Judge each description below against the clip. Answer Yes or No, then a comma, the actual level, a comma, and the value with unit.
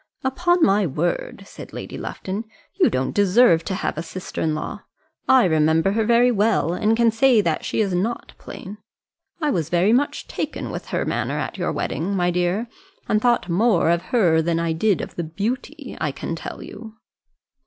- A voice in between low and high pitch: No, high, 195 Hz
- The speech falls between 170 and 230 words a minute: Yes, average, 190 wpm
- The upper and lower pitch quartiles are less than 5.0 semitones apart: No, wide, 5.6 semitones